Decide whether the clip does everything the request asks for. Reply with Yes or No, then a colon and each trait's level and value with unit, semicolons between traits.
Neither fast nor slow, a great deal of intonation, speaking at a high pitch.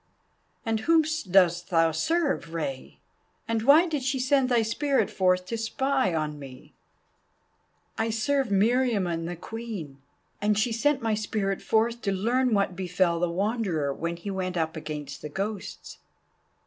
Yes: average, 150 wpm; wide, 5.7 semitones; high, 205 Hz